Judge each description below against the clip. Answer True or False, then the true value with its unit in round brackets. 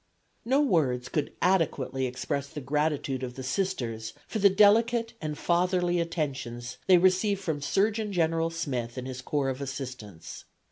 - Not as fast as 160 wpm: True (150 wpm)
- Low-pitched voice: False (155 Hz)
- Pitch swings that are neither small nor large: False (6.3 semitones)